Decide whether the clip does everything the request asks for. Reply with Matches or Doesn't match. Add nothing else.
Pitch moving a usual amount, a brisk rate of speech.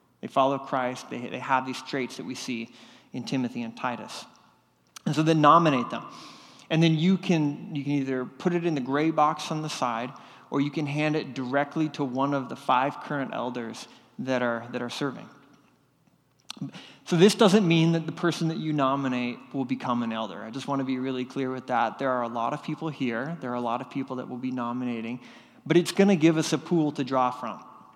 Matches